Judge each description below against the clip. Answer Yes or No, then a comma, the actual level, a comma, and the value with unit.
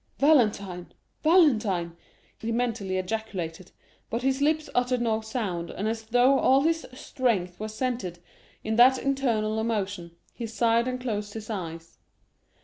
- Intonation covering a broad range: No, average, 4.4 semitones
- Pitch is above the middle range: Yes, high, 225 Hz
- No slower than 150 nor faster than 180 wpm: No, average, 140 wpm